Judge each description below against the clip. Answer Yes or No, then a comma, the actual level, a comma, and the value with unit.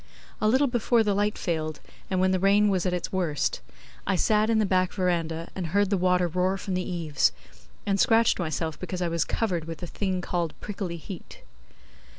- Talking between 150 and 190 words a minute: No, average, 200 wpm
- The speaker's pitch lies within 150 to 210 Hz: Yes, medium, 185 Hz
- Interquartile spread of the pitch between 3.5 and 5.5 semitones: No, average, 3.0 semitones